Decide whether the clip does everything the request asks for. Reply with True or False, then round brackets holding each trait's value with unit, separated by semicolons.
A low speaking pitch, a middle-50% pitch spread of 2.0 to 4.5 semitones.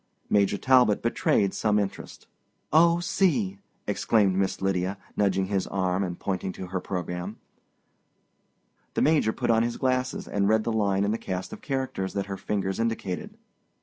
True (100 Hz; 3.2 semitones)